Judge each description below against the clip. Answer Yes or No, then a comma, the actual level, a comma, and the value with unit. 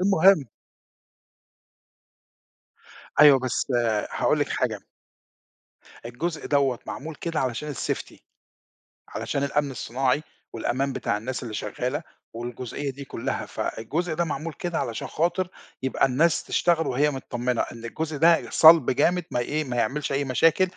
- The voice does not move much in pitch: No, average, 4.2 semitones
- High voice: No, medium, 140 Hz